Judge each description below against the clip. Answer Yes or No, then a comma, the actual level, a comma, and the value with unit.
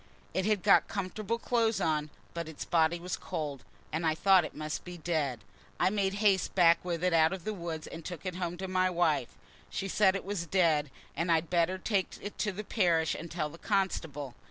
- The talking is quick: Yes, fast, 215 wpm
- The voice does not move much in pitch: No, average, 3.1 semitones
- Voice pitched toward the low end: No, medium, 175 Hz